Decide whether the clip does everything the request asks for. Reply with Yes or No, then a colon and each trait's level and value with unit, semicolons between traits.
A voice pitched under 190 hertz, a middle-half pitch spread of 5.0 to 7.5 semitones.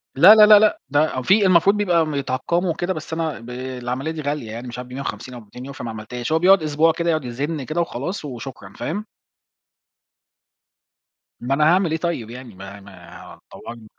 Yes: medium, 140 Hz; wide, 5.5 semitones